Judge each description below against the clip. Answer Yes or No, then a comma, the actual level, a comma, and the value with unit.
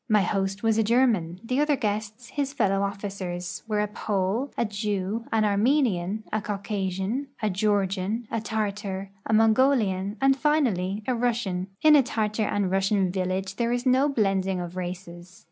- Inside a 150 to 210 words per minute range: Yes, average, 160 wpm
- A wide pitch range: No, average, 3.3 semitones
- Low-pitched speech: No, high, 210 Hz